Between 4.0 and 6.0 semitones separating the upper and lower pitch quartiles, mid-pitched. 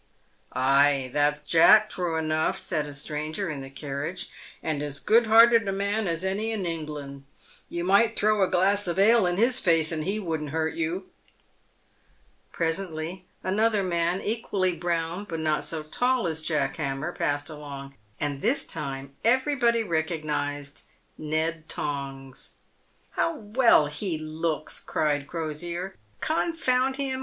Yes: average, 5.2 semitones; medium, 165 Hz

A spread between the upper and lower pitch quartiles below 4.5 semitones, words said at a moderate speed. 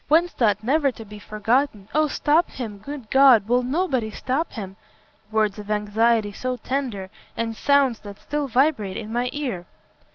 No: average, 4.8 semitones; average, 165 wpm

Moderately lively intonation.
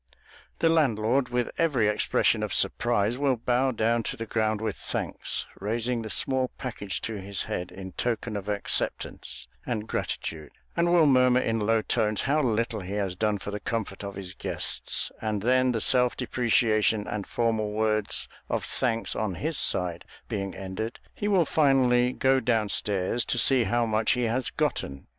Yes: average, 3.2 semitones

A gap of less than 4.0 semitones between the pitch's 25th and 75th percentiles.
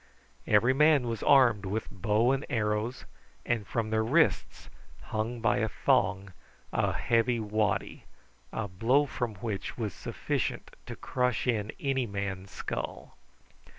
Yes: average, 2.9 semitones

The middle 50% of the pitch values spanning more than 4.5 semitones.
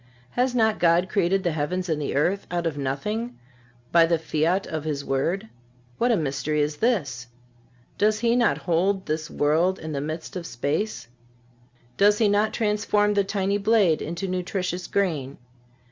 Yes: average, 5.0 semitones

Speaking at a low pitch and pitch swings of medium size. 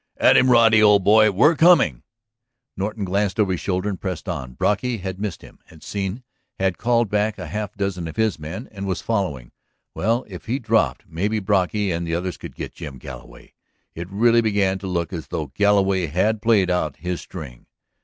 Yes: low, 100 Hz; average, 3.4 semitones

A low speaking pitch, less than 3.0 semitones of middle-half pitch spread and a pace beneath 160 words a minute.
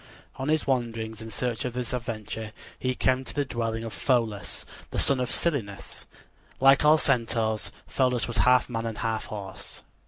No: low, 120 Hz; narrow, 2.4 semitones; average, 175 wpm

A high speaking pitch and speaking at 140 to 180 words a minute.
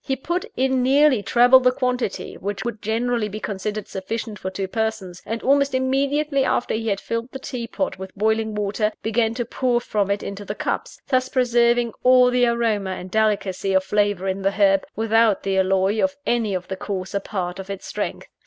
No: high, 220 Hz; average, 200 wpm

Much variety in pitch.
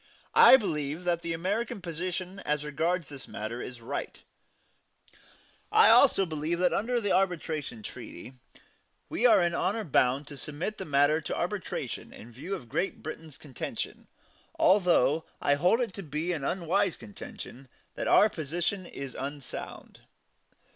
No: average, 4.5 semitones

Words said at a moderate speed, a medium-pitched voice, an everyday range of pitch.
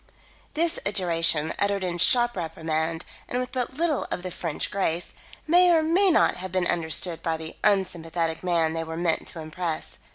No: average, 175 wpm; medium, 175 Hz; wide, 6.7 semitones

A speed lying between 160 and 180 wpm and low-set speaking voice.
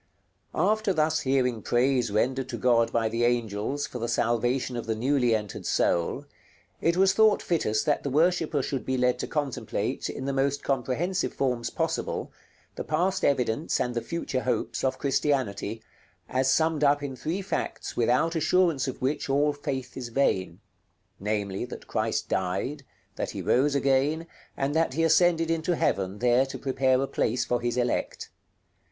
Yes: average, 170 wpm; low, 130 Hz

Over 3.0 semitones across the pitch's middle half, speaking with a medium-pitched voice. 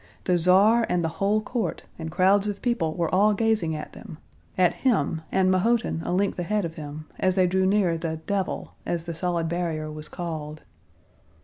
Yes: average, 3.7 semitones; medium, 180 Hz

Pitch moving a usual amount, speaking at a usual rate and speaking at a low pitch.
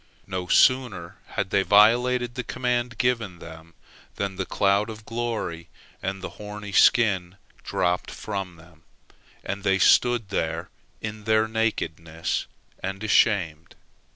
No: average, 4.0 semitones; slow, 125 wpm; low, 100 Hz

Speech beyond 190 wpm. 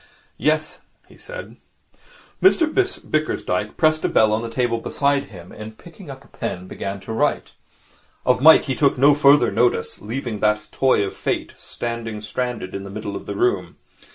No: average, 175 wpm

